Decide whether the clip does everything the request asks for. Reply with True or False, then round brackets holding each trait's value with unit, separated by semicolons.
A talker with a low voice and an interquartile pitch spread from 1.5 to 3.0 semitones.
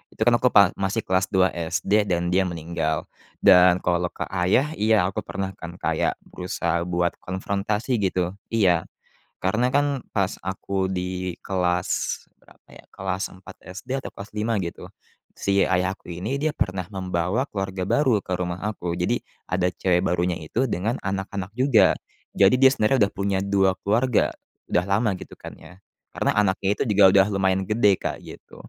True (95 Hz; 2.6 semitones)